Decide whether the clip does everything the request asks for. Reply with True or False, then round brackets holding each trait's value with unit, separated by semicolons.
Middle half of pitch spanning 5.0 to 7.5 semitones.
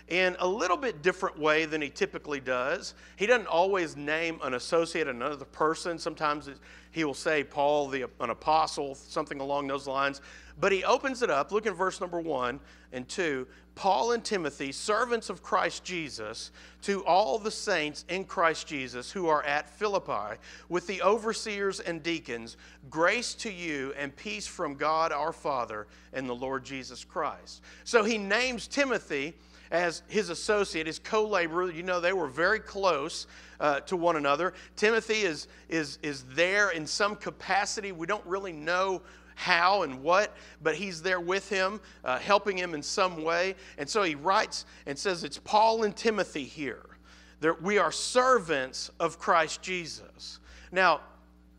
True (5.6 semitones)